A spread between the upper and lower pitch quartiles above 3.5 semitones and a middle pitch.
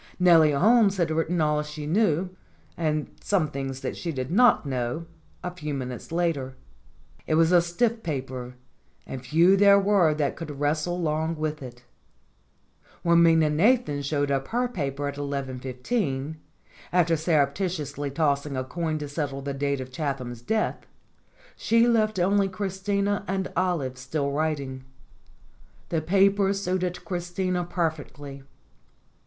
Yes: average, 4.6 semitones; medium, 155 Hz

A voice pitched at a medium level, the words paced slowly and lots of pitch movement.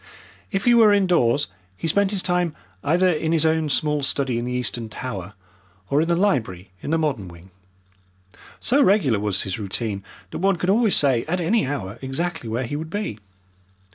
No: medium, 150 Hz; average, 190 wpm; wide, 7.4 semitones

